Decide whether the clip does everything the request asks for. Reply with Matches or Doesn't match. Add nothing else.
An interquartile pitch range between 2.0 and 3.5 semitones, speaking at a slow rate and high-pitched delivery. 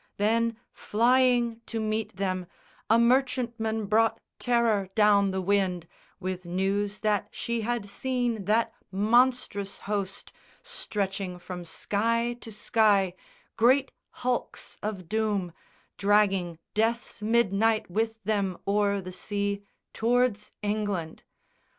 Matches